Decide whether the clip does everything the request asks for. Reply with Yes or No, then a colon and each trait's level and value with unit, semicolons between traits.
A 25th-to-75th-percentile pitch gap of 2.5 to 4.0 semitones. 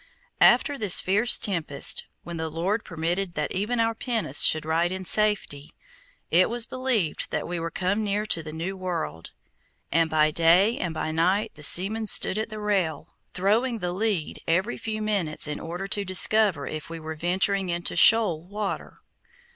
No: average, 4.5 semitones